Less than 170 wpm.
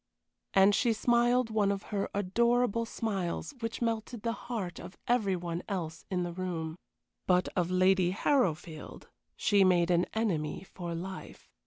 Yes: average, 150 wpm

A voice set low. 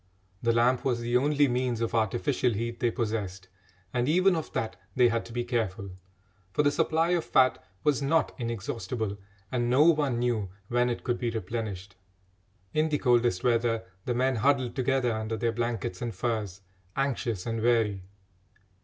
Yes: low, 120 Hz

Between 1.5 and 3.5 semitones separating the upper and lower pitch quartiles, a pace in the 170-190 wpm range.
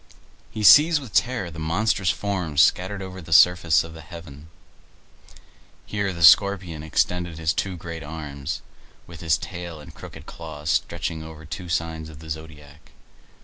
No: average, 2.8 semitones; average, 150 wpm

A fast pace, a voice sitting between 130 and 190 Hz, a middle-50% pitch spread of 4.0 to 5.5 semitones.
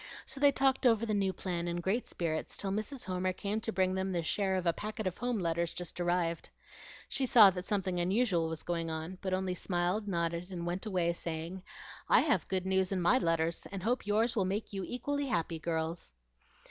No: fast, 210 wpm; medium, 185 Hz; average, 3.5 semitones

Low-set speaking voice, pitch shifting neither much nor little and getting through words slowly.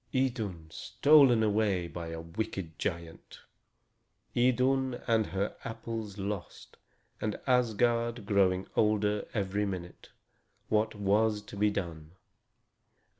Yes: low, 105 Hz; average, 3.4 semitones; slow, 105 wpm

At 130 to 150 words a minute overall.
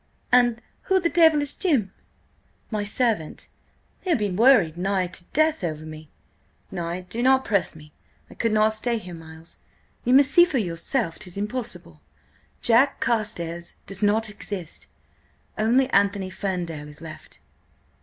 Yes: average, 145 wpm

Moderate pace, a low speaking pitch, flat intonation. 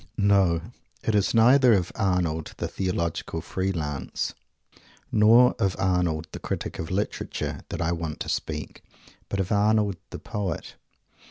No: average, 145 wpm; very low, 95 Hz; average, 3.8 semitones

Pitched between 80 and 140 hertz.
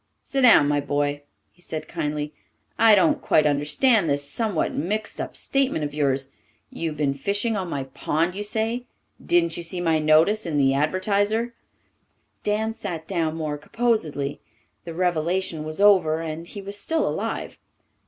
No: medium, 170 Hz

